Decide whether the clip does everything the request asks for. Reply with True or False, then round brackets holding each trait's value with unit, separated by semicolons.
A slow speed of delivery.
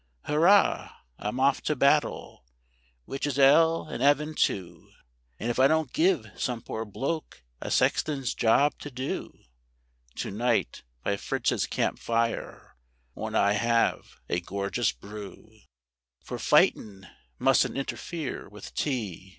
True (125 wpm)